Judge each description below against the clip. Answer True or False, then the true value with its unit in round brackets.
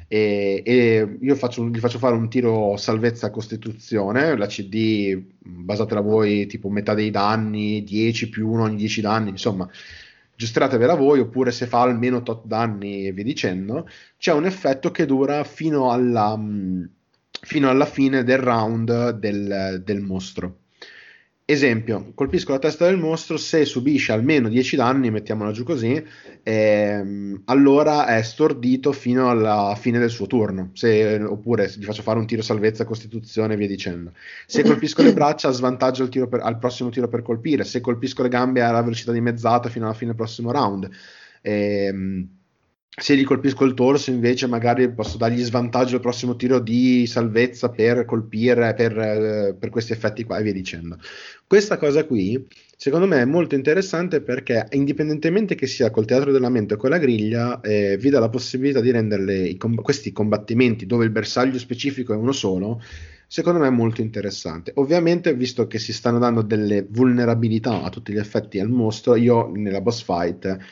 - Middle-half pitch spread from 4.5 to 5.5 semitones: False (3.3 semitones)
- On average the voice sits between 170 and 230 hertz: False (115 Hz)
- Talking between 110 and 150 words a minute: False (170 wpm)